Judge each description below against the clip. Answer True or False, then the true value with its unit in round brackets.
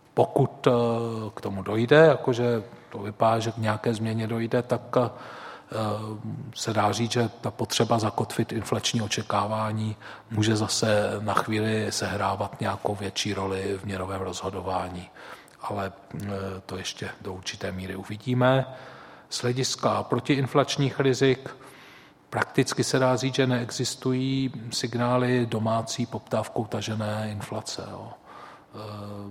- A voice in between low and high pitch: False (115 Hz)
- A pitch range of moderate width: True (3.1 semitones)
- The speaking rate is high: False (115 wpm)